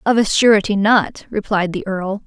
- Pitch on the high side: Yes, high, 205 Hz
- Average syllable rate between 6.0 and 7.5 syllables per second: No, 4.8 syllables/s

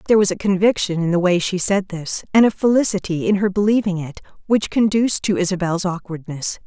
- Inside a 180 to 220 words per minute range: Yes, average, 200 wpm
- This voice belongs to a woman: Yes, female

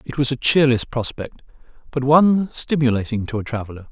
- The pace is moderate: Yes, average, 170 wpm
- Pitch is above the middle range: No, low, 130 Hz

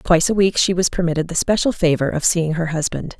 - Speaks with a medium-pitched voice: Yes, medium, 170 Hz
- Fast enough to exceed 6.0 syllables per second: Yes, 6.2 syllables/s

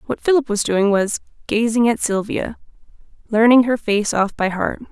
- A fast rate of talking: No, average, 160 wpm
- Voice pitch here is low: No, high, 220 Hz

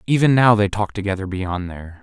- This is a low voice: Yes, low, 100 Hz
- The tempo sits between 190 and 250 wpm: Yes, fast, 205 wpm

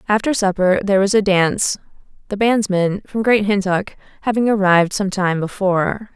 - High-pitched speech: Yes, high, 200 Hz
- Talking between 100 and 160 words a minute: Yes, average, 155 wpm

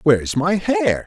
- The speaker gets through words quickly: No, average, 170 wpm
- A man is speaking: Yes, male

